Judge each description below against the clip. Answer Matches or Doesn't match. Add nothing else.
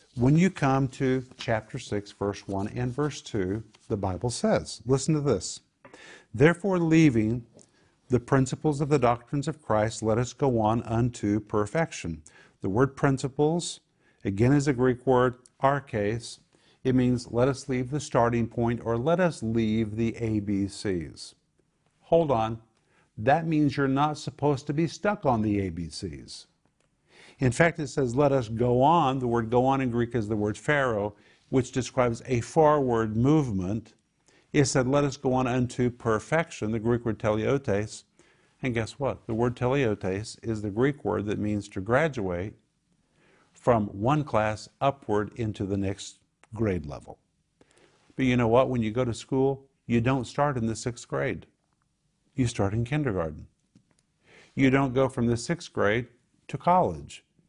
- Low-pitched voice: Matches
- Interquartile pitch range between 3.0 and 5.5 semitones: Matches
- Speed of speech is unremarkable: Matches